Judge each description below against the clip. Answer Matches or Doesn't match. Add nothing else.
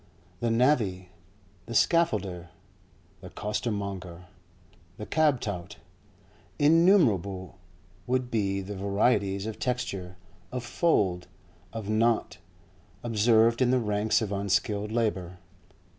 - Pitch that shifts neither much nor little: Matches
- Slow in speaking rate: Matches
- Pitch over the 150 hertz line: Doesn't match